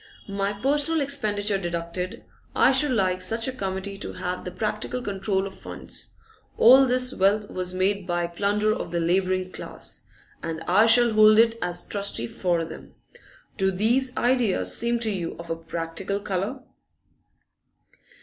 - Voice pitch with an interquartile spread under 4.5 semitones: Yes, average, 3.8 semitones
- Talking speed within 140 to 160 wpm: Yes, average, 155 wpm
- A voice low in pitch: No, high, 200 Hz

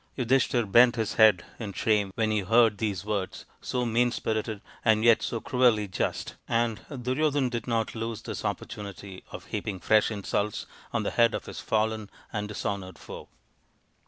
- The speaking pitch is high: No, low, 110 Hz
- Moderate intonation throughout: No, narrow, 2.3 semitones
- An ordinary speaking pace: Yes, average, 170 wpm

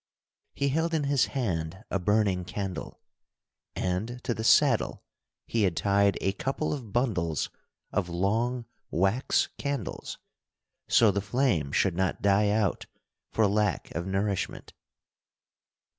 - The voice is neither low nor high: No, low, 100 Hz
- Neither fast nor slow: No, slow, 130 wpm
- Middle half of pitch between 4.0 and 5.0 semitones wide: Yes, average, 4.3 semitones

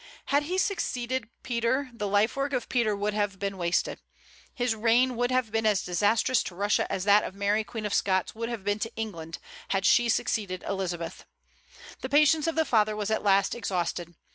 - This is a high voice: Yes, high, 215 Hz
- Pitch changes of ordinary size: Yes, average, 3.6 semitones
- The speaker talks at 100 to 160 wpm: No, average, 195 wpm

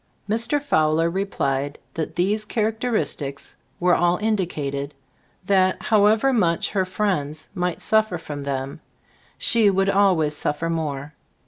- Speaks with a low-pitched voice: No, medium, 180 Hz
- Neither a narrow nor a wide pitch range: No, wide, 5.8 semitones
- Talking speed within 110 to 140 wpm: Yes, slow, 135 wpm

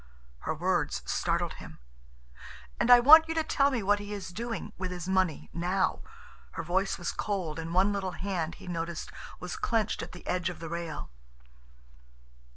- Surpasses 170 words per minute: No, average, 165 wpm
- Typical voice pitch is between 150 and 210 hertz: Yes, medium, 185 Hz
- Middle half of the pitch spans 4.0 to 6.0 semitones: No, average, 3.1 semitones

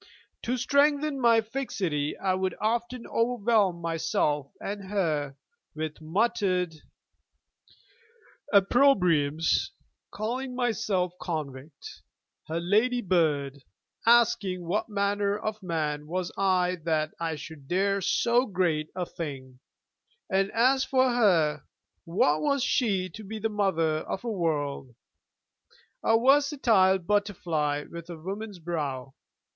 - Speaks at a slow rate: Yes, slow, 115 wpm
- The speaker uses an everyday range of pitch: No, wide, 5.9 semitones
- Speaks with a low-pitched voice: No, medium, 185 Hz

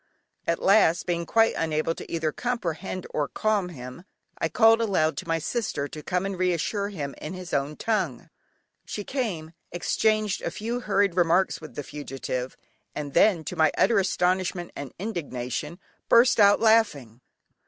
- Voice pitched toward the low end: No, medium, 180 Hz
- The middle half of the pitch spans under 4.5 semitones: No, average, 5.1 semitones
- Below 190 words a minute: Yes, average, 160 wpm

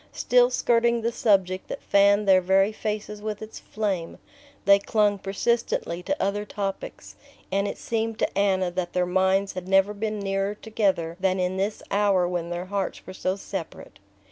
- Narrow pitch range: Yes, narrow, 2.2 semitones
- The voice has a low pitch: No, high, 200 Hz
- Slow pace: No, average, 170 wpm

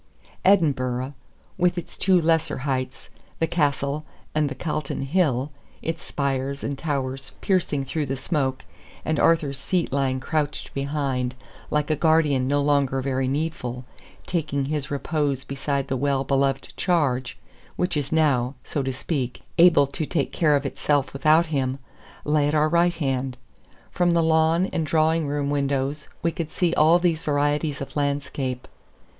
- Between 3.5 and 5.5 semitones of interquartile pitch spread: No, average, 2.9 semitones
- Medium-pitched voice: Yes, medium, 145 Hz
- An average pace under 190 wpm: Yes, average, 155 wpm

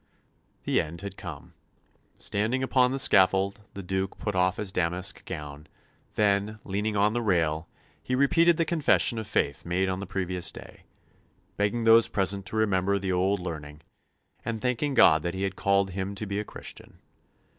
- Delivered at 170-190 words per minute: Yes, average, 175 wpm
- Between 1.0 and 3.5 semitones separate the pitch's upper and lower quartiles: Yes, average, 2.9 semitones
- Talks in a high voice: No, low, 100 Hz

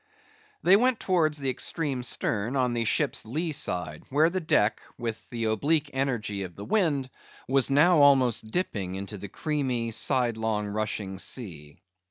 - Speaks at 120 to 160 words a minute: Yes, average, 155 wpm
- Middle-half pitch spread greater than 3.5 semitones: Yes, wide, 5.6 semitones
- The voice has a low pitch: Yes, low, 125 Hz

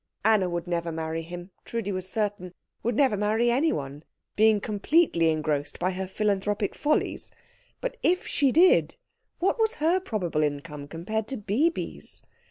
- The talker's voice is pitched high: Yes, high, 205 Hz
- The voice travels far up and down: Yes, wide, 6.0 semitones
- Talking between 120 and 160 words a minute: Yes, average, 150 wpm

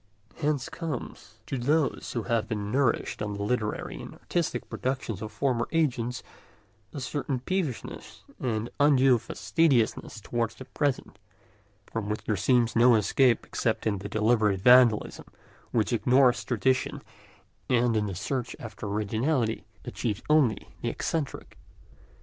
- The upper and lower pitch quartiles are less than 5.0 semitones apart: Yes, average, 3.7 semitones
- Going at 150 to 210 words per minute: No, slow, 135 wpm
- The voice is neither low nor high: No, low, 120 Hz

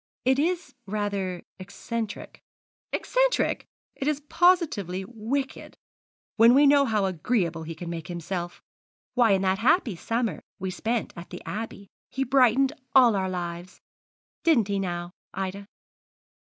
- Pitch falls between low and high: No, high, 205 Hz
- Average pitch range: No, wide, 6.1 semitones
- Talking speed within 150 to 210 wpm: No, slow, 135 wpm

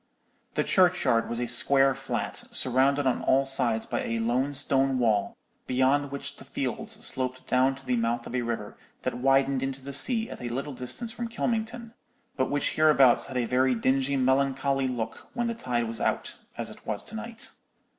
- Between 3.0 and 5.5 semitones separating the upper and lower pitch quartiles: No, narrow, 2.4 semitones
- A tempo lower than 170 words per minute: No, average, 190 wpm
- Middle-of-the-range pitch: No, low, 130 Hz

